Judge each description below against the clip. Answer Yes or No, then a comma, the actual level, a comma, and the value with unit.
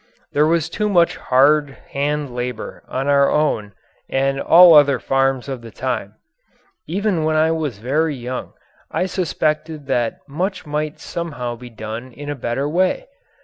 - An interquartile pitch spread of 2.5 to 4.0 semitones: Yes, average, 3.7 semitones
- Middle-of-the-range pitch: Yes, medium, 145 Hz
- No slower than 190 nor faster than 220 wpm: No, average, 145 wpm